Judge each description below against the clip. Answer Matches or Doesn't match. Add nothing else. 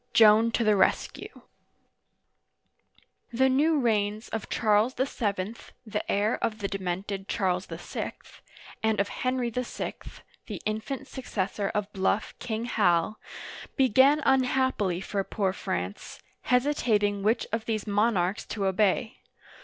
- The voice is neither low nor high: Doesn't match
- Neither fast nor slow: Doesn't match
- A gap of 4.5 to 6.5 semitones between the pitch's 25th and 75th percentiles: Doesn't match